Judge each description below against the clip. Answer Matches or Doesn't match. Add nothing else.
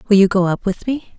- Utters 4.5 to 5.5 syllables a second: Doesn't match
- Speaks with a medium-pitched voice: Doesn't match